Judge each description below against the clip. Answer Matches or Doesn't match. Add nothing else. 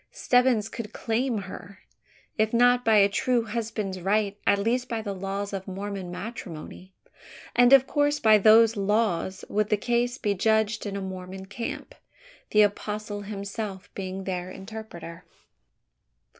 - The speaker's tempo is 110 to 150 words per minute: Matches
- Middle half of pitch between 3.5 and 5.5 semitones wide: Doesn't match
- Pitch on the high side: Matches